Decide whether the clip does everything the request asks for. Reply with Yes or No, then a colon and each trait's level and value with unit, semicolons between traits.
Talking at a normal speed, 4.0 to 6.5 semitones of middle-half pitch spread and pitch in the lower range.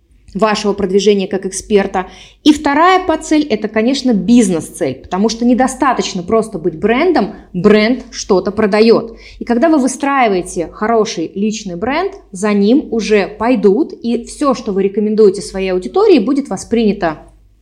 No: average, 135 wpm; average, 4.7 semitones; high, 215 Hz